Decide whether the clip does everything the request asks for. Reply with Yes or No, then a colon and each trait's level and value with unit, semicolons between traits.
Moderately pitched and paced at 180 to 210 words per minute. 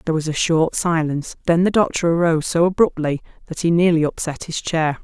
Yes: medium, 165 Hz; average, 200 wpm